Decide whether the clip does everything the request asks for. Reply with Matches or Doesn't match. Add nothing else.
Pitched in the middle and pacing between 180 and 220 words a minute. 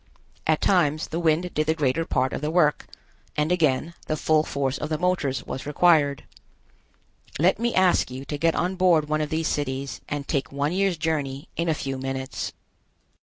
Matches